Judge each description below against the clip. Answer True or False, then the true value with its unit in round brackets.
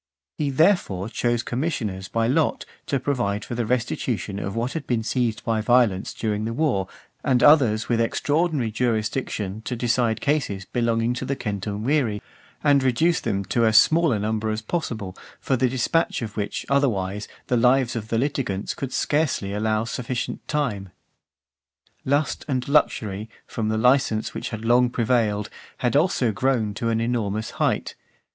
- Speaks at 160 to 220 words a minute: True (165 wpm)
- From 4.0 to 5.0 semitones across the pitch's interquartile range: False (3.5 semitones)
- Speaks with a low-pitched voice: True (115 Hz)